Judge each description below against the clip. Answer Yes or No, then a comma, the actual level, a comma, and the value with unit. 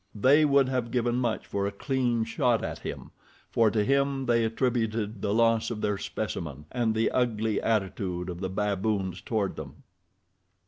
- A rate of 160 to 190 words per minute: Yes, average, 170 wpm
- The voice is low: Yes, low, 110 Hz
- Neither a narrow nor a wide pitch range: Yes, average, 3.2 semitones